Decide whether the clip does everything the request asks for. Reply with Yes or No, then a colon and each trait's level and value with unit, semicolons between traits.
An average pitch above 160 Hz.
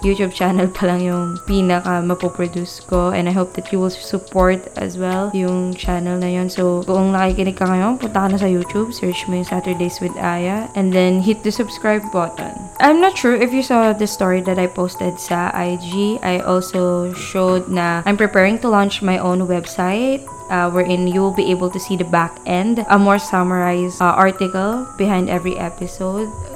Yes: medium, 185 Hz